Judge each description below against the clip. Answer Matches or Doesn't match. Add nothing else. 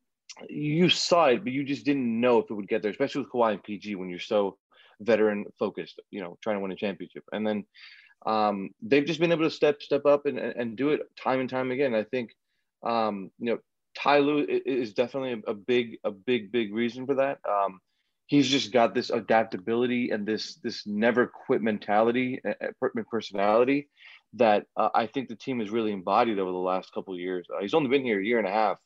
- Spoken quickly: Matches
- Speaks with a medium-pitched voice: Doesn't match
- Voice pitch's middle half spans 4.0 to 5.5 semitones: Matches